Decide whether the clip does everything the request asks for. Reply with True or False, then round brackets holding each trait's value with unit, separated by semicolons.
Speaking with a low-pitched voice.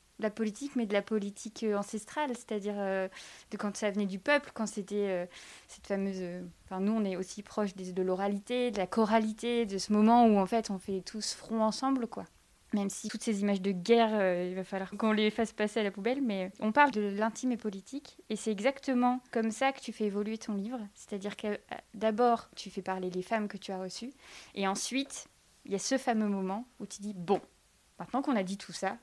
False (210 Hz)